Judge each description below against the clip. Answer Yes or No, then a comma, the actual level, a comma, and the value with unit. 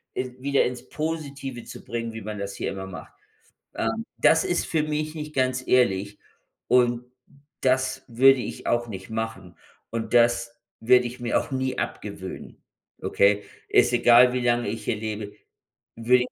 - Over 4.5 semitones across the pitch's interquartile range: No, narrow, 2.6 semitones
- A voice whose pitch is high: No, low, 120 Hz